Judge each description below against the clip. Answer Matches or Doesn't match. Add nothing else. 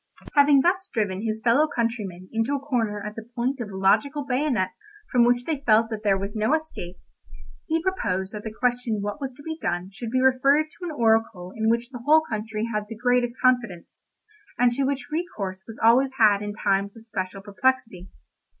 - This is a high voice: Matches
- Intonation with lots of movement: Doesn't match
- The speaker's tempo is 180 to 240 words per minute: Matches